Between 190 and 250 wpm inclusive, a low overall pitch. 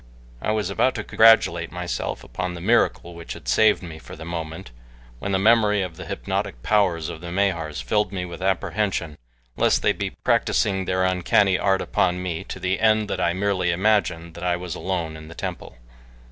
Yes: average, 195 wpm; very low, 90 Hz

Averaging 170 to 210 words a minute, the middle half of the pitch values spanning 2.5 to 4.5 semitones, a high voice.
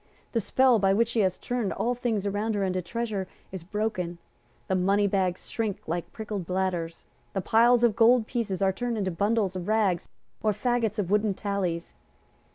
Yes: average, 180 wpm; average, 3.3 semitones; high, 205 Hz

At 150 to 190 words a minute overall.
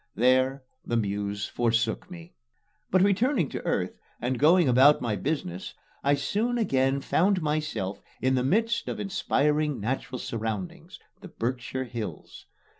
No: slow, 135 wpm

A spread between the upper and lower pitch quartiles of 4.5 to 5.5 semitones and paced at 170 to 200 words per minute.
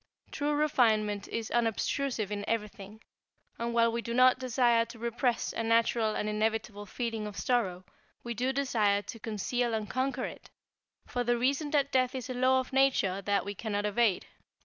No: average, 3.2 semitones; average, 175 wpm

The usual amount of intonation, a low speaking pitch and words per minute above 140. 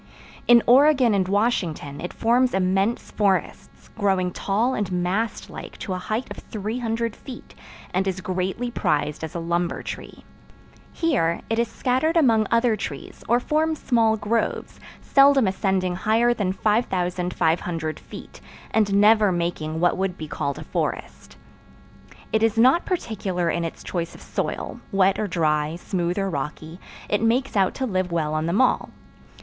No: average, 4.7 semitones; high, 195 Hz; average, 155 wpm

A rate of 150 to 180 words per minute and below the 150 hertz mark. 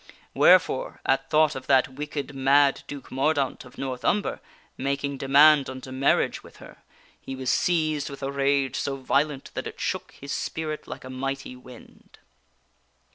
Yes: average, 160 wpm; medium, 140 Hz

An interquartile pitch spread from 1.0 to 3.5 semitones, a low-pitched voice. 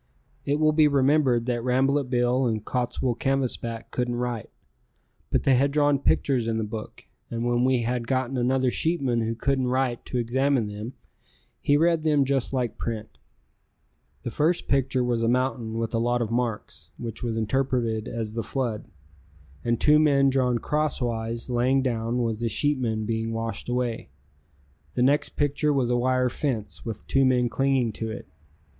Yes: average, 2.8 semitones; low, 125 Hz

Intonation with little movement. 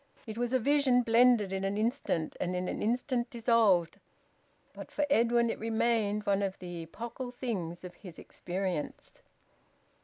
No: average, 4.3 semitones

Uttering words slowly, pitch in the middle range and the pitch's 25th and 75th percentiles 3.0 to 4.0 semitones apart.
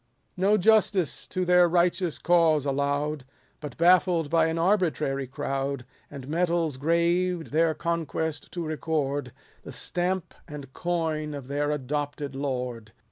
Yes: slow, 130 wpm; medium, 160 Hz; average, 3.5 semitones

